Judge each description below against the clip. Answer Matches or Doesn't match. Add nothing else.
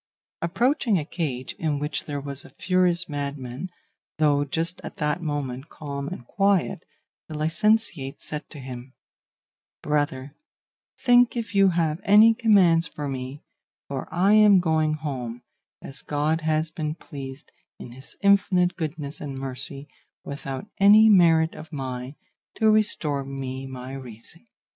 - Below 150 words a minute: Matches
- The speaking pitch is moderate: Matches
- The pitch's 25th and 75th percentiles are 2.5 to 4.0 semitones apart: Doesn't match